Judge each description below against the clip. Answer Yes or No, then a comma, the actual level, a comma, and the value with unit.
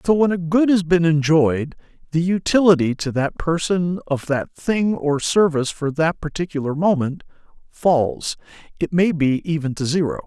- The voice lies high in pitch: No, medium, 160 Hz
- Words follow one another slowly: No, average, 165 wpm